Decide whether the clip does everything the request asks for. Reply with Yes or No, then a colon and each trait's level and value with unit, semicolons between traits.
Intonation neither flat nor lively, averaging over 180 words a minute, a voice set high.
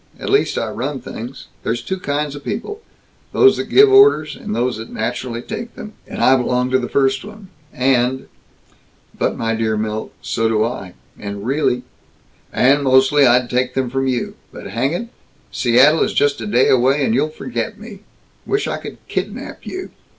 No: average, 4.3 semitones; average, 190 wpm; low, 130 Hz